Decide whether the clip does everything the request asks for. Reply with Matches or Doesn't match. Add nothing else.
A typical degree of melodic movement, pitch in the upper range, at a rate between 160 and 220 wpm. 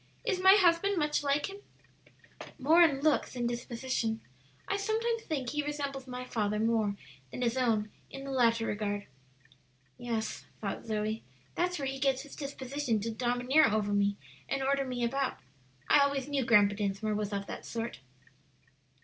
Matches